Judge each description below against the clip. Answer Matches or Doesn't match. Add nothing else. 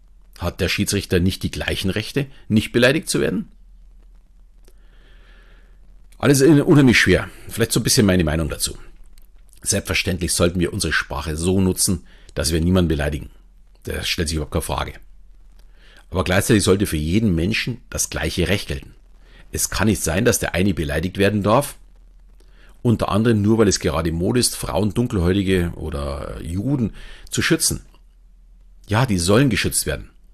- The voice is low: Matches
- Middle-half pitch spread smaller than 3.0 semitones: Doesn't match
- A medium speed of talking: Matches